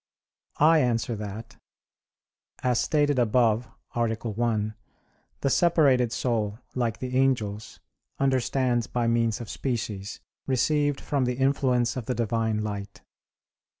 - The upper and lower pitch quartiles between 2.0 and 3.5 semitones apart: Yes, average, 2.8 semitones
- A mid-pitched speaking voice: No, low, 120 Hz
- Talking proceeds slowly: Yes, slow, 115 wpm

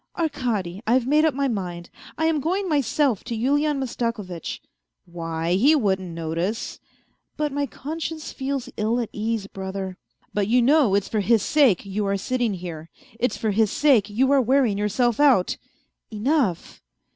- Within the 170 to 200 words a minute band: Yes, average, 180 wpm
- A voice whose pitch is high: Yes, high, 230 Hz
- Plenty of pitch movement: Yes, wide, 6.2 semitones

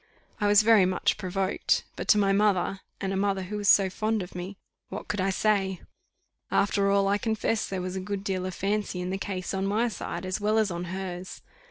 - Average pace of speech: No, fast, 225 wpm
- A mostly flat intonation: Yes, narrow, 1.8 semitones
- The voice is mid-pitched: No, high, 195 Hz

